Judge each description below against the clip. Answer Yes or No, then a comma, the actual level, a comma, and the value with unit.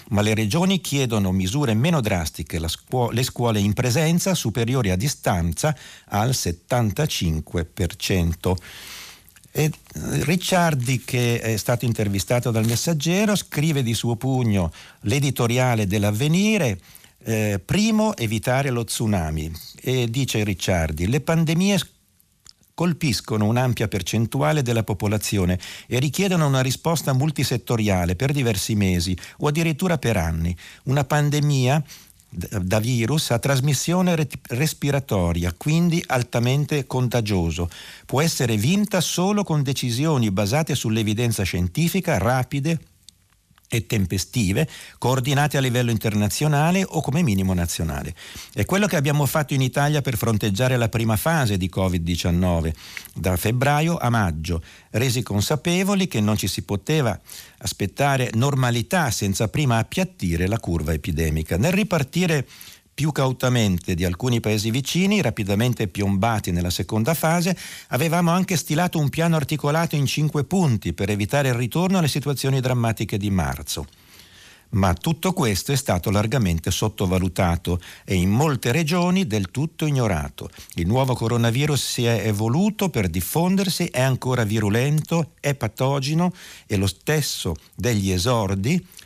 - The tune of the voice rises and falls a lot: Yes, wide, 6.8 semitones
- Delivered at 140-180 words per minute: No, average, 125 wpm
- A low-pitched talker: Yes, low, 120 Hz